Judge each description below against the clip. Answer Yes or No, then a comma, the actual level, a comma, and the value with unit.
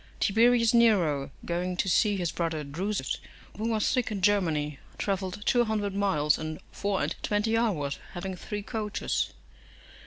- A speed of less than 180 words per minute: Yes, average, 150 wpm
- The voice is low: No, high, 200 Hz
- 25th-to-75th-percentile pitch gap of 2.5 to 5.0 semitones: Yes, average, 4.1 semitones